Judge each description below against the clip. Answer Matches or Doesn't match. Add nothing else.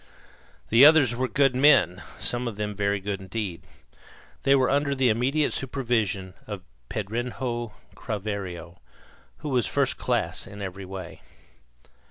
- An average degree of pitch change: Matches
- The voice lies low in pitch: Matches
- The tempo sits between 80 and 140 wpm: Matches